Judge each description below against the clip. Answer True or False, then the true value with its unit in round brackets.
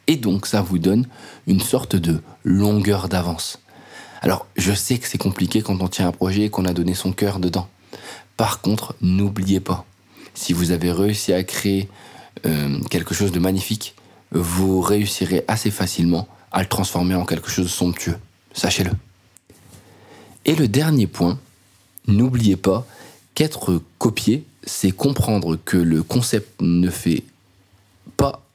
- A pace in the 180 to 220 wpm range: False (150 wpm)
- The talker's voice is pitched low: True (95 Hz)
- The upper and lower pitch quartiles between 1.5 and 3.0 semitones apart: True (2.5 semitones)